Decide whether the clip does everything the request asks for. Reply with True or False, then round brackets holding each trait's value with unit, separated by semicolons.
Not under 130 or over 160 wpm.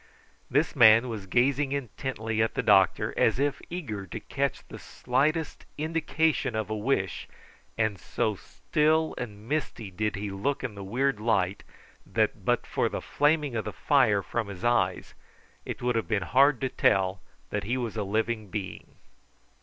False (170 wpm)